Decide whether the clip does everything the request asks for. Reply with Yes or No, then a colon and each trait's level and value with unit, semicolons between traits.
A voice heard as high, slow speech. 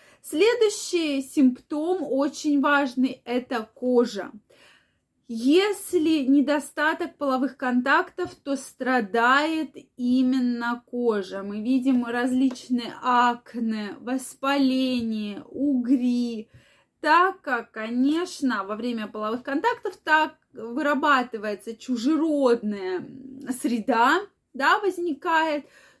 Yes: very high, 265 Hz; slow, 75 wpm